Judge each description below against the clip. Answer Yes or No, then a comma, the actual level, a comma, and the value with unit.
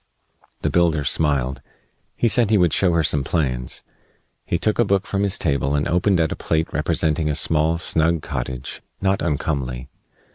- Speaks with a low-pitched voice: Yes, very low, 80 Hz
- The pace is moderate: Yes, average, 175 wpm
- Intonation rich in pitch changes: No, average, 4.1 semitones